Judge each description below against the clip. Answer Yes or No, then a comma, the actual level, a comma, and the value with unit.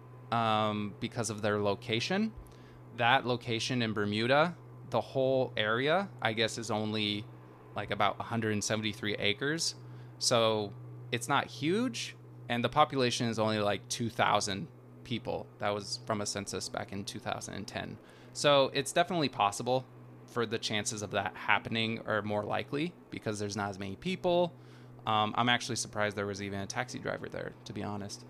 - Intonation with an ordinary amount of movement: Yes, average, 3.4 semitones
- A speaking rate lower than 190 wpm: Yes, average, 155 wpm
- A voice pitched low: Yes, low, 110 Hz